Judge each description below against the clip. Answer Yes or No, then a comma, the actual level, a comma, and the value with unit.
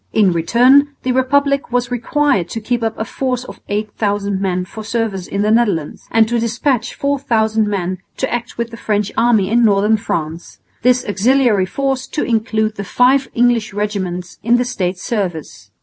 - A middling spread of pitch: Yes, average, 3.6 semitones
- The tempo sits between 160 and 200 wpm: Yes, average, 175 wpm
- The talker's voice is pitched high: Yes, high, 225 Hz